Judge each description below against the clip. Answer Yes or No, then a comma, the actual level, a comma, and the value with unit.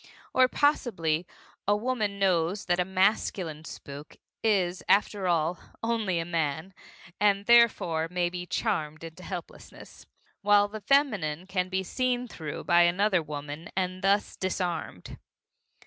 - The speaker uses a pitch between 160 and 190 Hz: Yes, medium, 185 Hz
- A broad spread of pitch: No, average, 3.8 semitones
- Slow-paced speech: Yes, slow, 130 wpm